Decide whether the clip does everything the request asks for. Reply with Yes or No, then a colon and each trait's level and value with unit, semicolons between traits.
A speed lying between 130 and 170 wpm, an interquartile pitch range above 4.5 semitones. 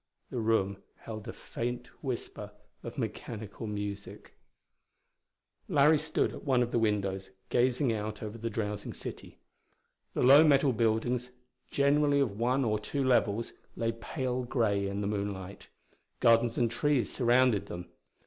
No: average, 140 wpm; average, 3.5 semitones